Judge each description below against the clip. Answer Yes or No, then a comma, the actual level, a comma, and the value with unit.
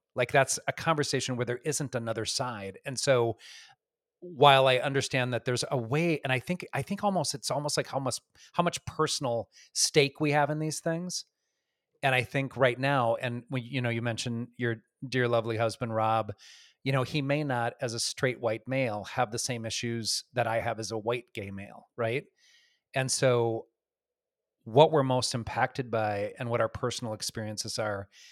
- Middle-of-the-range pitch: No, low, 125 Hz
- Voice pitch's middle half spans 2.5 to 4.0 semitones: Yes, average, 3.7 semitones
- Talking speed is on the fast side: No, average, 190 wpm